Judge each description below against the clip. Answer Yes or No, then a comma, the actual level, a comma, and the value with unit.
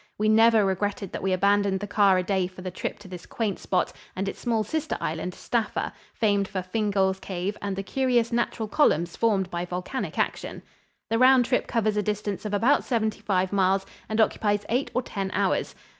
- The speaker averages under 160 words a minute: No, average, 200 wpm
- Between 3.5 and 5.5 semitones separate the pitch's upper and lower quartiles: No, average, 2.9 semitones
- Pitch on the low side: No, high, 205 Hz